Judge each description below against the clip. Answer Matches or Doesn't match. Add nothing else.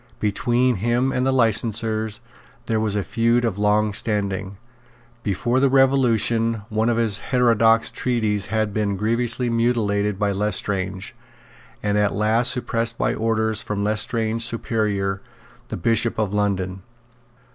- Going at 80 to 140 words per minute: Matches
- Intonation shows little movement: Matches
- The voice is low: Matches